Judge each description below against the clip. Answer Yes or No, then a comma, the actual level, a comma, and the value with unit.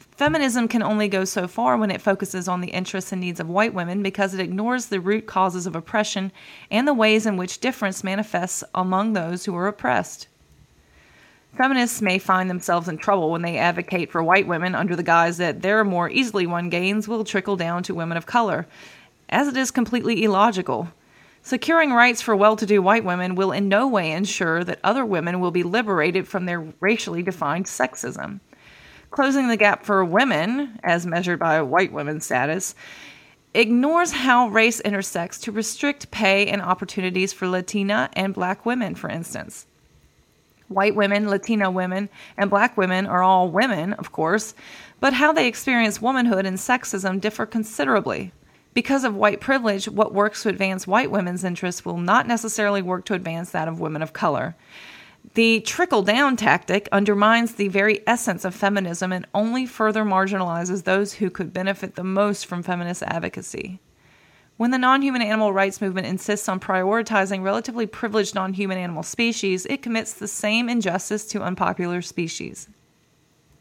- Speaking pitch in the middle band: No, high, 200 Hz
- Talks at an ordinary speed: Yes, average, 170 wpm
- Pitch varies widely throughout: No, average, 3.2 semitones